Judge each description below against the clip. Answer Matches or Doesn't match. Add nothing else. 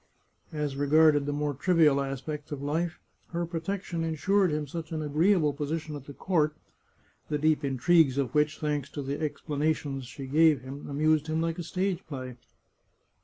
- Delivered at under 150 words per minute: Doesn't match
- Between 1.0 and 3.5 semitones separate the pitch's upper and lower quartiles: Matches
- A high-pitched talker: Doesn't match